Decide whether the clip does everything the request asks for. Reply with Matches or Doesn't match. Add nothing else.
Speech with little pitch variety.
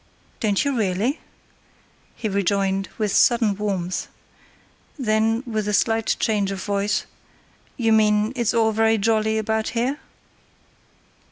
Matches